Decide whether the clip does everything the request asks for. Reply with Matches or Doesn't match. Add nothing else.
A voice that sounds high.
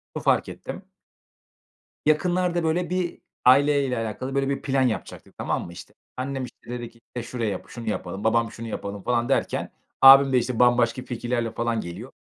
Doesn't match